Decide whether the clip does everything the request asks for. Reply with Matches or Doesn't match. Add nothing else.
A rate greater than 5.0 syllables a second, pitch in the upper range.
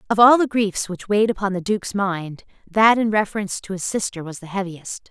Matches